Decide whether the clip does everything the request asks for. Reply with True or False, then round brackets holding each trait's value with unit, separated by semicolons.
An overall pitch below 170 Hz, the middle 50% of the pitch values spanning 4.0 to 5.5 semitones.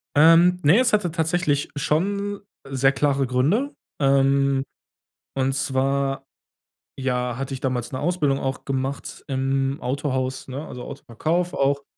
False (140 Hz; 3.1 semitones)